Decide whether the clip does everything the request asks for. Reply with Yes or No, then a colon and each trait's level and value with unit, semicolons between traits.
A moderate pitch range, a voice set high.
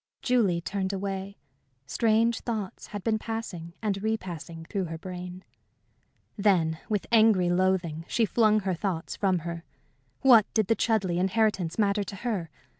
Yes: average, 3.6 semitones; high, 195 Hz